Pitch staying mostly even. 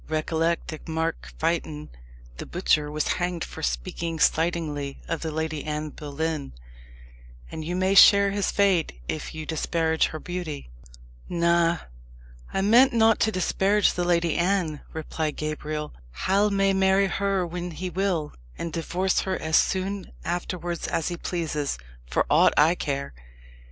No: average, 3.1 semitones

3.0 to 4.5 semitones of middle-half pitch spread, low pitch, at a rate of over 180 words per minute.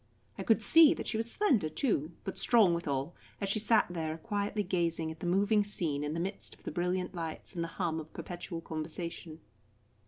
No: average, 4.2 semitones; medium, 175 Hz; average, 200 wpm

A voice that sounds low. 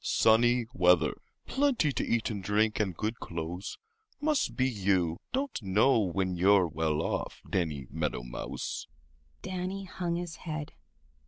Yes: low, 105 Hz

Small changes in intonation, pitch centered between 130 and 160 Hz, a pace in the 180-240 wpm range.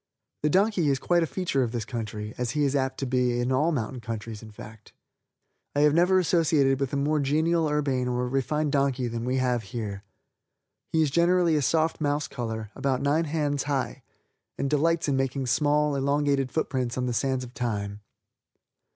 No: average, 3.4 semitones; low, 135 Hz; average, 195 wpm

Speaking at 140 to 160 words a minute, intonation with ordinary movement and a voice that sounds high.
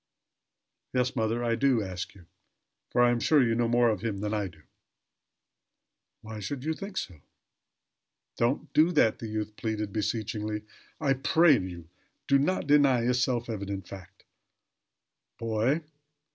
No: average, 150 wpm; average, 3.7 semitones; low, 115 Hz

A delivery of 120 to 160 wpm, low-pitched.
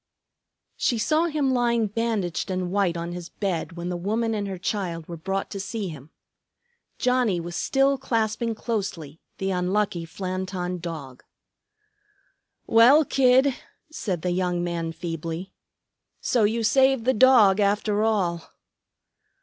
No: slow, 135 wpm; high, 195 Hz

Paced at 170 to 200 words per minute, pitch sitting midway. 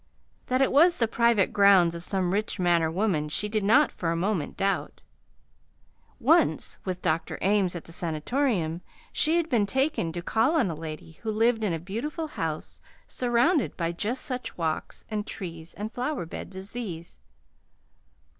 No: average, 175 wpm; high, 200 Hz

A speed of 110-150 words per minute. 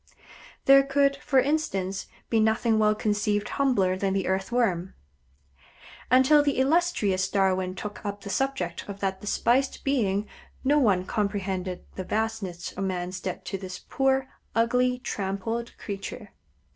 Yes: slow, 135 wpm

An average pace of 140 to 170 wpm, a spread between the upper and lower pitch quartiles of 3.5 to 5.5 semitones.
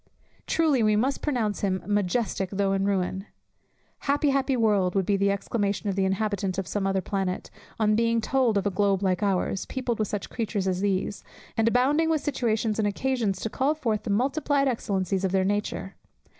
No: average, 190 wpm; average, 3.8 semitones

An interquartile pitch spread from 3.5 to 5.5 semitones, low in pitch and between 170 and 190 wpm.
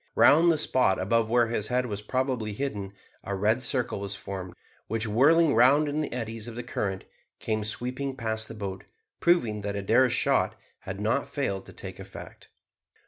Yes: average, 4.0 semitones; low, 115 Hz; average, 180 wpm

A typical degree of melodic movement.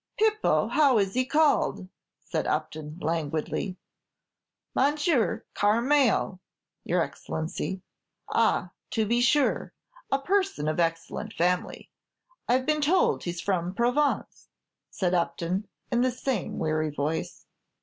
No: wide, 8.1 semitones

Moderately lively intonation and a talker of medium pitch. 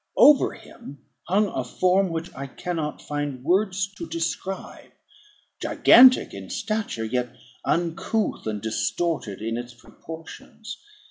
No: wide, 7.7 semitones; medium, 165 Hz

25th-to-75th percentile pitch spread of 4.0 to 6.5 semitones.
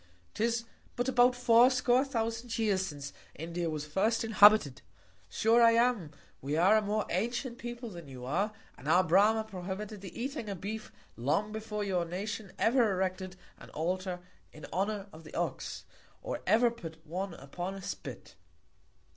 Yes: average, 4.7 semitones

